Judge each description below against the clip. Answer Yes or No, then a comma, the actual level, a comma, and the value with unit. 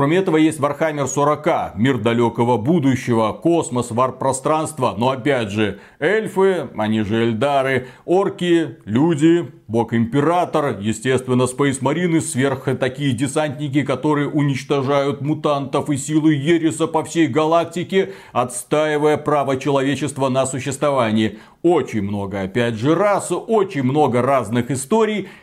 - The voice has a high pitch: No, medium, 140 Hz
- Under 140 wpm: Yes, average, 120 wpm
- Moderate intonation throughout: Yes, average, 3.9 semitones